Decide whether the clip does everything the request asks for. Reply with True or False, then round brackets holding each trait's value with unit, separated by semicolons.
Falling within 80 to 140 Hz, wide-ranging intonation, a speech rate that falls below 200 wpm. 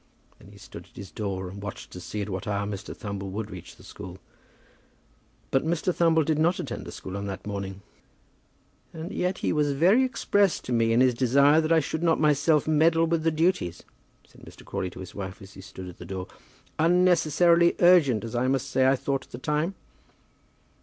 False (135 Hz; 8.3 semitones; 205 wpm)